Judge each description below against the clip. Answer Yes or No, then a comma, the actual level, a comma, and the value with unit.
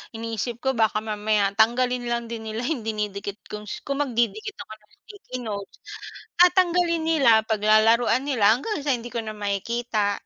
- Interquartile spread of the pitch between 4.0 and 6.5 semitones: No, average, 3.2 semitones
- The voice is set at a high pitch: Yes, high, 230 Hz